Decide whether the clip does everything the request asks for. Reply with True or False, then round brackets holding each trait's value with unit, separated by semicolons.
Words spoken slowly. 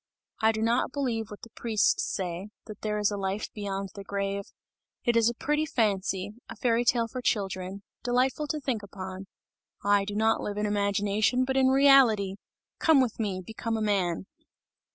False (180 wpm)